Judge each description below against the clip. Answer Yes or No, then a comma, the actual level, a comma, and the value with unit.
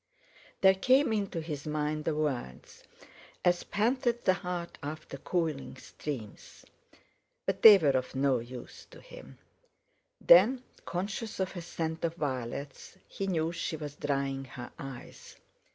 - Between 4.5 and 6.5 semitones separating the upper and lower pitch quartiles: Yes, wide, 5.5 semitones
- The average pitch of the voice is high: No, medium, 160 Hz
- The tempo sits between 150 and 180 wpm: No, slow, 135 wpm